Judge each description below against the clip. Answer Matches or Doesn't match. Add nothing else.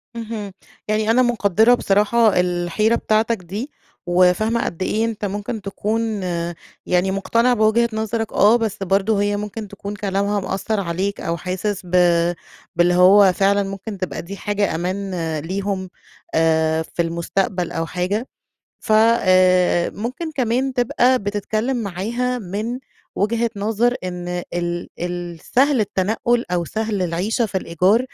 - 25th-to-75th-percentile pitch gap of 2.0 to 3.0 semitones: Doesn't match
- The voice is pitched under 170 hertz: Doesn't match